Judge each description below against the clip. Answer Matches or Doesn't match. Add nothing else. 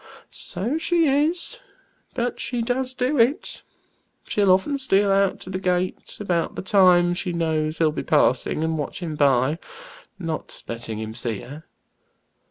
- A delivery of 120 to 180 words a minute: Matches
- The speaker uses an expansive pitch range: Matches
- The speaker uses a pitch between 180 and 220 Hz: Matches